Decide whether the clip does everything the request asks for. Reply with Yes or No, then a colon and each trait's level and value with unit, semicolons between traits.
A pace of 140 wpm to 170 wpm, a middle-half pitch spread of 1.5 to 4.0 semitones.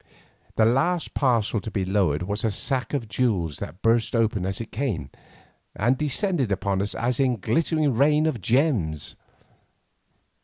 No: average, 155 wpm; wide, 5.5 semitones